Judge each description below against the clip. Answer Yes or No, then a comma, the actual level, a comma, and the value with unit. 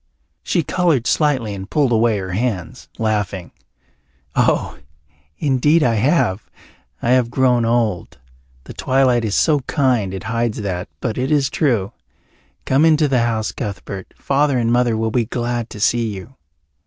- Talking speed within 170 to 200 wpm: No, average, 155 wpm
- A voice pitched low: Yes, low, 120 Hz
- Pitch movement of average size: Yes, average, 3.7 semitones